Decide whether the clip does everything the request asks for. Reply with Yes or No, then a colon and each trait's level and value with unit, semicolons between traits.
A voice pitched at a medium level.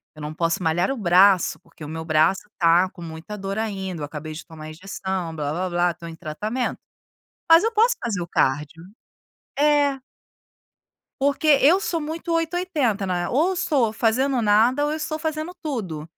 No: high, 195 Hz